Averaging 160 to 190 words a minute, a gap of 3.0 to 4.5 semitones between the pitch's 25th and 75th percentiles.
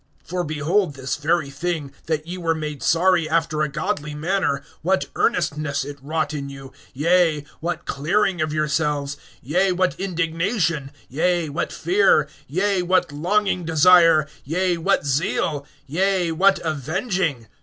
No: average, 140 wpm; average, 3.5 semitones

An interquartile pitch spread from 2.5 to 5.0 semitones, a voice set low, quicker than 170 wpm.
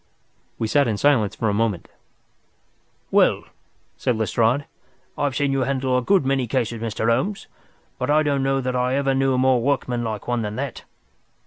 Yes: average, 3.1 semitones; low, 130 Hz; average, 180 wpm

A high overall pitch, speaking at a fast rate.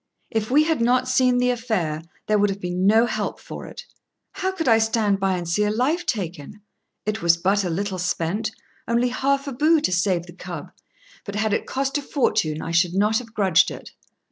Yes: high, 215 Hz; fast, 215 wpm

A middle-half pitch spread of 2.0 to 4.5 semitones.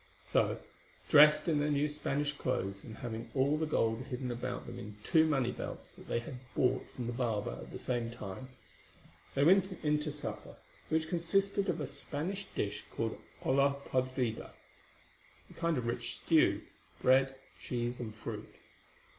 Yes: average, 4.1 semitones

